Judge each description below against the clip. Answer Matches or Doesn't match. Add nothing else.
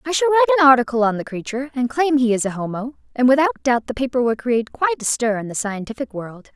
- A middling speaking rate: Doesn't match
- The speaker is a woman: Matches